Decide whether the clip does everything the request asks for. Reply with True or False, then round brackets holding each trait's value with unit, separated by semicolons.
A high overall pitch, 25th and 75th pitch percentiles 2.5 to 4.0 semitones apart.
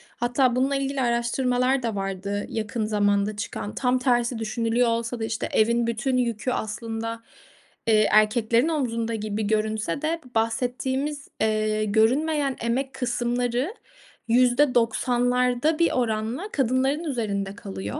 True (235 Hz; 2.8 semitones)